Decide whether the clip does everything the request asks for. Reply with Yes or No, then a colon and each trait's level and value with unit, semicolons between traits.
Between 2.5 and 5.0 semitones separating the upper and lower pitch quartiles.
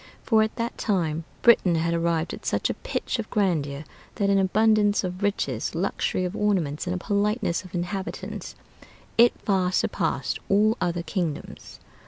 Yes: average, 3.7 semitones